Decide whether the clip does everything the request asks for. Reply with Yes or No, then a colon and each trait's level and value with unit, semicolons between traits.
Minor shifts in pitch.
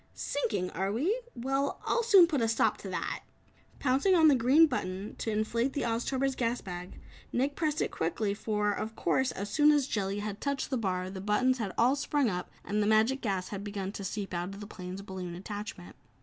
No: wide, 5.5 semitones